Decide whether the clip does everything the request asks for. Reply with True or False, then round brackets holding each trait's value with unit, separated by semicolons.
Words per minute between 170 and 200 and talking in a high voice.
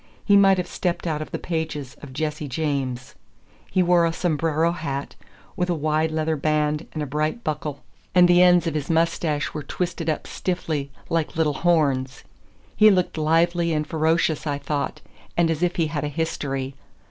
False (180 wpm; 155 Hz)